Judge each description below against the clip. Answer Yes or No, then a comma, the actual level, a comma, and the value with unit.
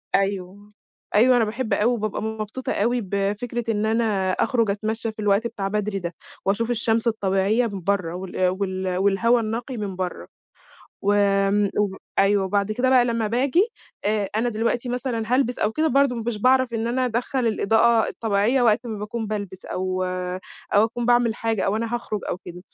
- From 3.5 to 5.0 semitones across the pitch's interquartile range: No, average, 2.9 semitones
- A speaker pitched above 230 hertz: No, high, 215 Hz